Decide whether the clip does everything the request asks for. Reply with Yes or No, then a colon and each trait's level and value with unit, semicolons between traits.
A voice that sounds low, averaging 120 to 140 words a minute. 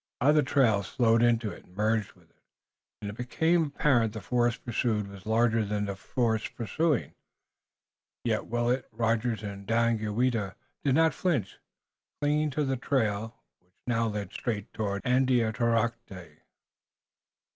Yes: low, 115 Hz; slow, 135 wpm